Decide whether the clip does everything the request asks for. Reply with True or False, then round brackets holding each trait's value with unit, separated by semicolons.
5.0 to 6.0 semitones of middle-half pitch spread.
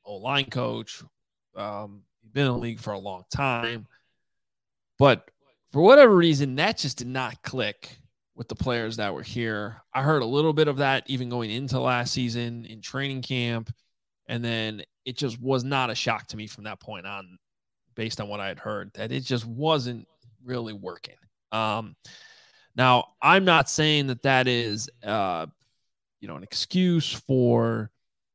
False (3.4 semitones)